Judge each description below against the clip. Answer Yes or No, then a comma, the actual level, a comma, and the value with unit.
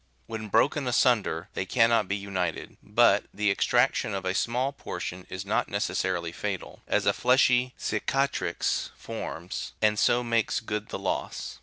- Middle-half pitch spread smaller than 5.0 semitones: Yes, average, 4.1 semitones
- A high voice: No, low, 110 Hz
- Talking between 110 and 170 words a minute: Yes, average, 160 wpm